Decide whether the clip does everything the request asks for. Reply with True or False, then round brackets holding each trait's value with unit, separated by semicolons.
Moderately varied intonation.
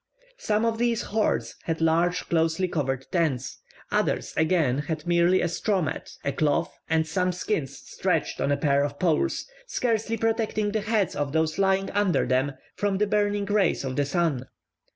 False (5.7 semitones)